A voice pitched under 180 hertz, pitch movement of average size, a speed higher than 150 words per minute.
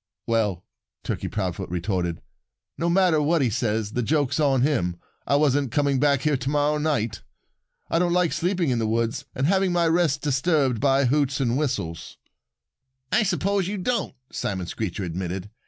No: medium, 140 Hz; wide, 5.9 semitones; average, 170 wpm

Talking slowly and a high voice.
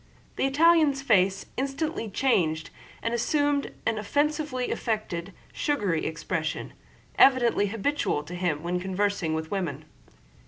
Yes: slow, 115 wpm; high, 210 Hz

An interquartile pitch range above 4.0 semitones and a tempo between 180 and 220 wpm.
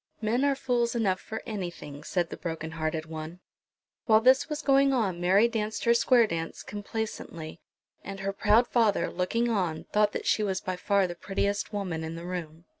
Yes: average, 4.9 semitones; average, 190 wpm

